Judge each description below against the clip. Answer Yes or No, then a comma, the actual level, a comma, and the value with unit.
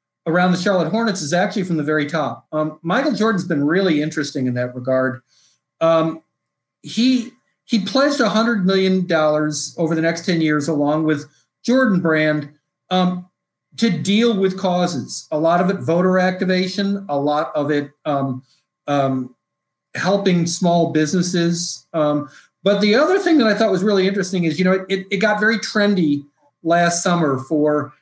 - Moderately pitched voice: Yes, medium, 170 Hz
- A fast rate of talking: No, average, 165 wpm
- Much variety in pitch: No, average, 4.5 semitones